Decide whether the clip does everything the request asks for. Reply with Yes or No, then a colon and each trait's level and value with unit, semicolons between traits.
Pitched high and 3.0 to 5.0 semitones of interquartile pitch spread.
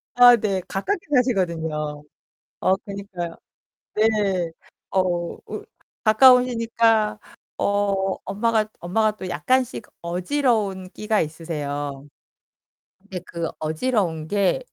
Yes: high, 195 Hz; average, 4.7 semitones